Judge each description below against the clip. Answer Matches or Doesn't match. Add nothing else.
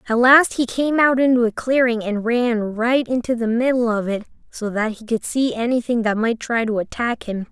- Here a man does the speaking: Doesn't match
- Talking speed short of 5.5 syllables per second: Matches